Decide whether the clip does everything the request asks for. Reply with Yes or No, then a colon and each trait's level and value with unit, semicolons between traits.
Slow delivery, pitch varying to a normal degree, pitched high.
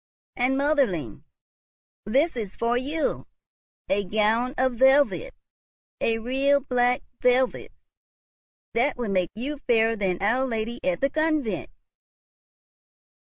Yes: slow, 115 wpm; average, 3.8 semitones; high, 245 Hz